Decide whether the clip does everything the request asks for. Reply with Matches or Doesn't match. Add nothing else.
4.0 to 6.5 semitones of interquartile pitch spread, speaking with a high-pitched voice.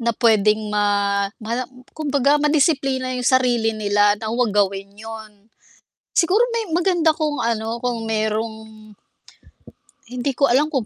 Matches